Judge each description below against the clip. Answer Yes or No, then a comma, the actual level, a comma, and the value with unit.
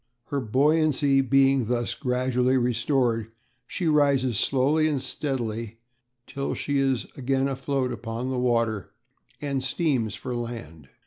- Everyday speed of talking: No, slow, 125 wpm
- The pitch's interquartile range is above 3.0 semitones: No, narrow, 2.6 semitones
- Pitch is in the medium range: No, low, 130 Hz